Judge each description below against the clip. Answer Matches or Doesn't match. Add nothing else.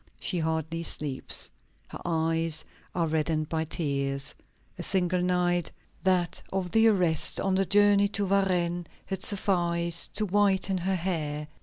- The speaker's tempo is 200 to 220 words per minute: Doesn't match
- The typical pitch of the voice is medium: Matches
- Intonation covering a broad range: Doesn't match